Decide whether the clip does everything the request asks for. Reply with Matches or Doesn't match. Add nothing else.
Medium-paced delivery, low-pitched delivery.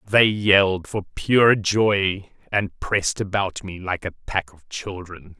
Matches